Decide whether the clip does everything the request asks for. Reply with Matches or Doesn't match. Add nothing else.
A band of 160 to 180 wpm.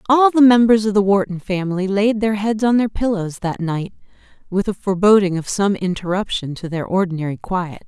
Doesn't match